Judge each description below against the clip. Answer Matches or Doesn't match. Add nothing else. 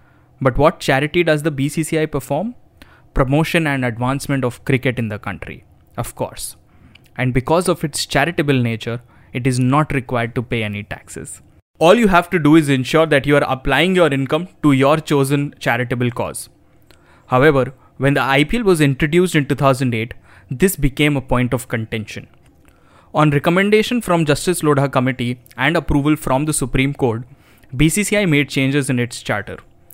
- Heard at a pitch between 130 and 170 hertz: Matches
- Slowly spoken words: Doesn't match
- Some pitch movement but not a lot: Matches